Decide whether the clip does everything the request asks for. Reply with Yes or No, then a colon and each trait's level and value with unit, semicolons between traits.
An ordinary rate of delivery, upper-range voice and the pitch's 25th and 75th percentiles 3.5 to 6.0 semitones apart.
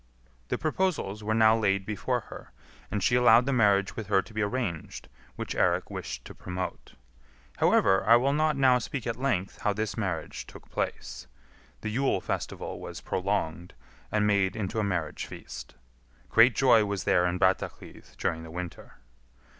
No: average, 170 wpm; low, 105 Hz; average, 4.0 semitones